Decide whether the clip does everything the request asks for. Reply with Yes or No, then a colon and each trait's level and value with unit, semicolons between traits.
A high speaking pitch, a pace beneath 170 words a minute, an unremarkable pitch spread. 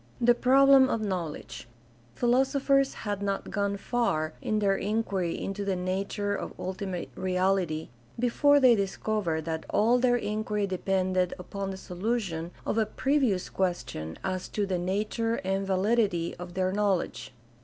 Yes: high, 195 Hz; average, 150 wpm; average, 3.6 semitones